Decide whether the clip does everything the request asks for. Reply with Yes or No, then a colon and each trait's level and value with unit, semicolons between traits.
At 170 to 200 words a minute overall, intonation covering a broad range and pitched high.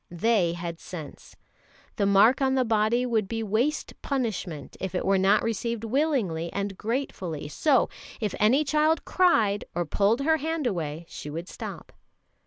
No: average, 160 wpm; wide, 6.1 semitones; high, 215 Hz